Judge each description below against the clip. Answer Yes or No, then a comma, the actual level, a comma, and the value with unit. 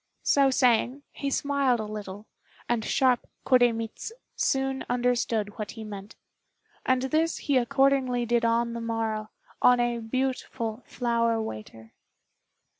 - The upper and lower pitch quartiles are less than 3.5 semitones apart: Yes, average, 2.7 semitones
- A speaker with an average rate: No, slow, 125 wpm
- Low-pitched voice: No, high, 240 Hz